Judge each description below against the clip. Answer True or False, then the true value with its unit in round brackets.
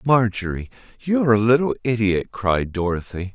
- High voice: False (105 Hz)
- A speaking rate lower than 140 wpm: True (125 wpm)